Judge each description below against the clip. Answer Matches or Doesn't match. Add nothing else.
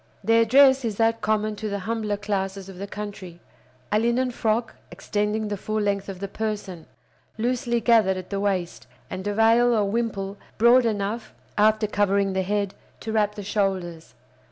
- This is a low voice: Doesn't match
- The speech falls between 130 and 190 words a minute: Matches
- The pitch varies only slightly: Matches